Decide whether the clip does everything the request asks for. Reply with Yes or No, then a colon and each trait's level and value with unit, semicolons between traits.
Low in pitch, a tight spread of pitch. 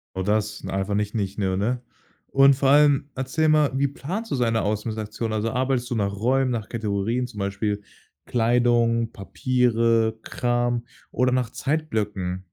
No: low, 115 Hz; average, 3.4 semitones